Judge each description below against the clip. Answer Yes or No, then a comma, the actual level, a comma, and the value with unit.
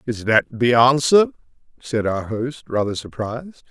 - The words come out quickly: No, average, 145 wpm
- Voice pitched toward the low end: Yes, low, 125 Hz